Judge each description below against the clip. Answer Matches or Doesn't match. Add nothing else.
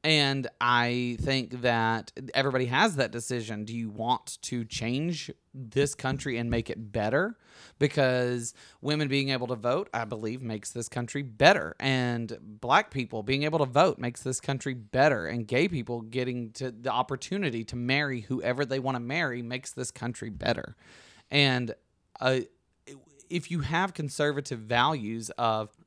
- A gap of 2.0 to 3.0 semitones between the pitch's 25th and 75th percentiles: Matches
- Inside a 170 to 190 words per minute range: Doesn't match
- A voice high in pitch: Doesn't match